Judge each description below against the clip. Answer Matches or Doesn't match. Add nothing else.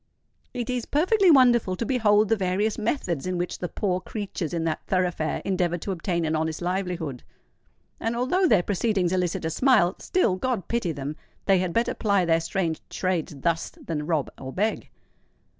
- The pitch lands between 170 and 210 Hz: Matches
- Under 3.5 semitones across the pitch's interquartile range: Doesn't match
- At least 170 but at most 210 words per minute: Matches